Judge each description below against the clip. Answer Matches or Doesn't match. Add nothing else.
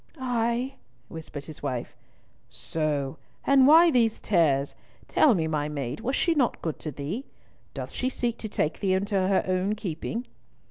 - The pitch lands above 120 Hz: Matches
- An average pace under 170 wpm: Matches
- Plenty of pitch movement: Matches